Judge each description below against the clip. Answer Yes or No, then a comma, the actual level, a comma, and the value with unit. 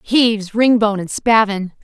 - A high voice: Yes, high, 215 Hz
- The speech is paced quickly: No, slow, 130 wpm